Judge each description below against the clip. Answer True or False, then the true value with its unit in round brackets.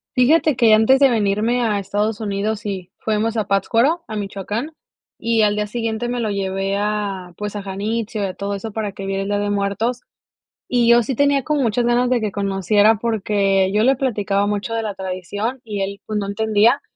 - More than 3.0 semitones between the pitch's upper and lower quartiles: False (2.7 semitones)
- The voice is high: True (210 Hz)